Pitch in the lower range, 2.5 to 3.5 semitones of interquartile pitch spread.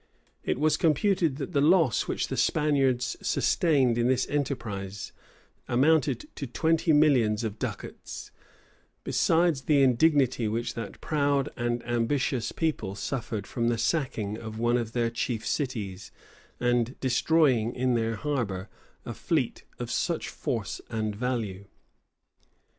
No: low, 125 Hz; average, 4.3 semitones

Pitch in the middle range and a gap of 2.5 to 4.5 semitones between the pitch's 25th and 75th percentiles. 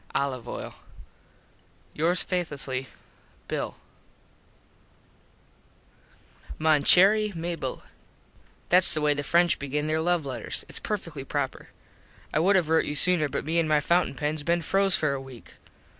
Yes: medium, 155 Hz; average, 3.5 semitones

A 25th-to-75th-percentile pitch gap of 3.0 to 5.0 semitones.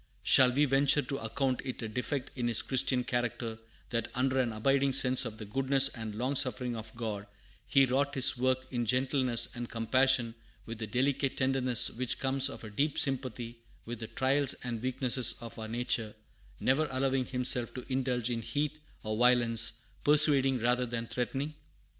No: narrow, 2.4 semitones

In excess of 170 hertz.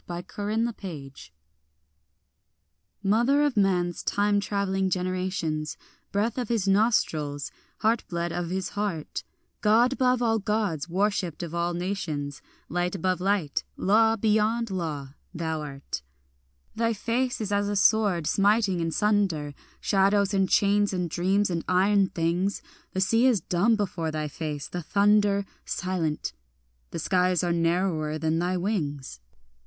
Yes: high, 190 Hz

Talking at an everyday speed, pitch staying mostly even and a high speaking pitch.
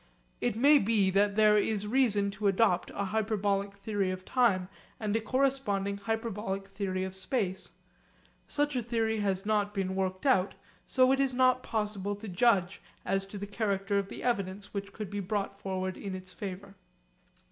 Yes: average, 175 wpm; narrow, 2.3 semitones; high, 200 Hz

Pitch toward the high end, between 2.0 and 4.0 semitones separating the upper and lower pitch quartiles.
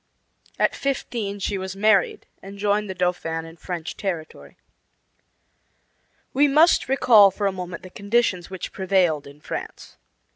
Yes: high, 195 Hz; average, 2.8 semitones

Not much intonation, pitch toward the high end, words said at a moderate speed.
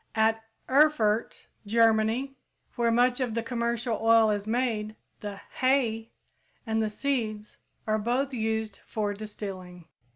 No: narrow, 2.1 semitones; high, 225 Hz; slow, 125 wpm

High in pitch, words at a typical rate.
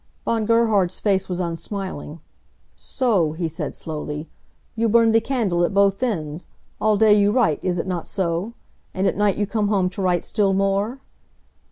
Yes: high, 195 Hz; average, 175 wpm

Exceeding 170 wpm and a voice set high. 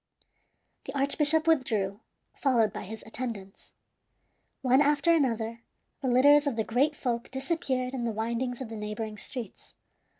No: average, 140 wpm; very high, 250 Hz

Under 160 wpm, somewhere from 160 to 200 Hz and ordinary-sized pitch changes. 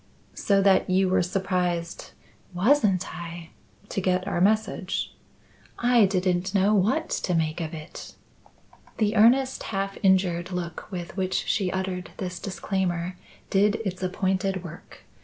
No: average, 140 wpm; high, 190 Hz; narrow, 1.9 semitones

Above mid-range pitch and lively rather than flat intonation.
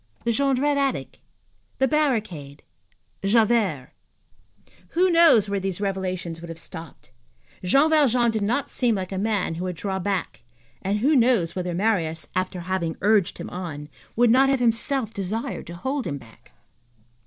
Yes: high, 200 Hz; wide, 5.7 semitones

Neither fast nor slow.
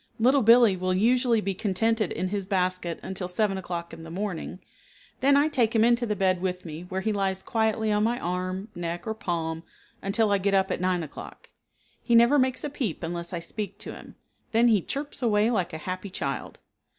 No: fast, 210 wpm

